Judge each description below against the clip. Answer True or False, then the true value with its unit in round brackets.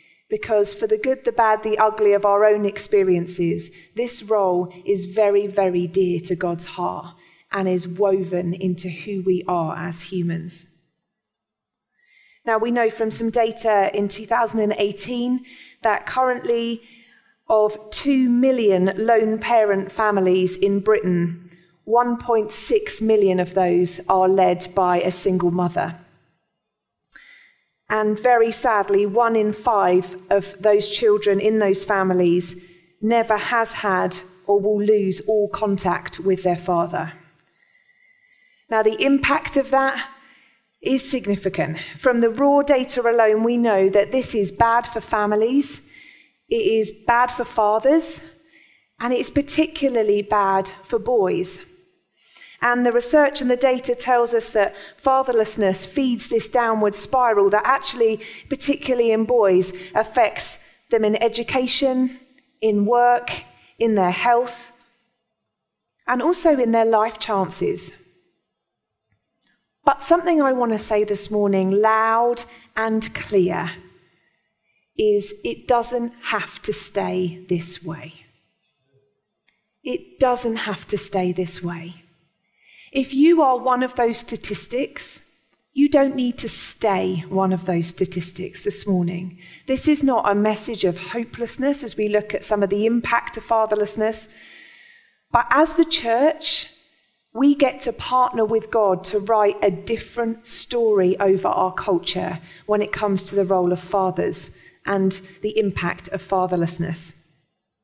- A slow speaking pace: True (130 wpm)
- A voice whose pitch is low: False (215 Hz)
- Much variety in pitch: False (4.3 semitones)